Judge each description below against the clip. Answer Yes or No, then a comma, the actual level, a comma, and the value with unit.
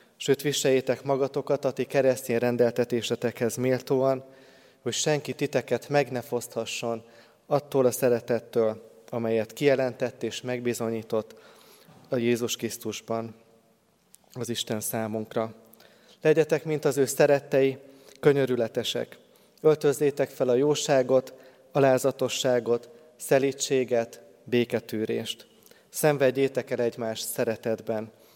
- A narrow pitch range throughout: No, average, 3.0 semitones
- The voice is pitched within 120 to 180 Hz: Yes, low, 125 Hz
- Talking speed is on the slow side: Yes, slow, 95 wpm